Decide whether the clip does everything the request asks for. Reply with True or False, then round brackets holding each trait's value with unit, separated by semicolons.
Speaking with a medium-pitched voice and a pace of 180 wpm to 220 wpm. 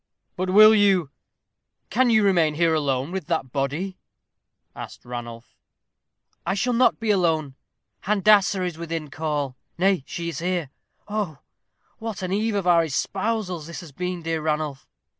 False (175 Hz; 150 wpm)